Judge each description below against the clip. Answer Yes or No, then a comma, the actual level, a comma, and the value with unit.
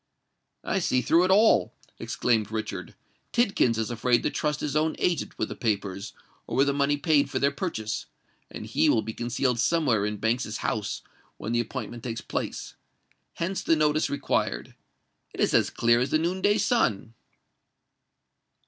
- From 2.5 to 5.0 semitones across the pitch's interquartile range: No, wide, 5.6 semitones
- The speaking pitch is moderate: No, low, 125 Hz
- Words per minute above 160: Yes, average, 170 wpm